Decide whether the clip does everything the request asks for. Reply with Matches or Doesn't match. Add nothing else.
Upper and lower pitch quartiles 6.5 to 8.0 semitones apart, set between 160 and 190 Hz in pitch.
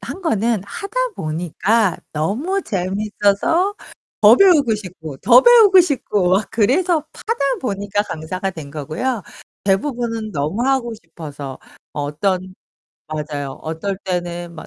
Doesn't match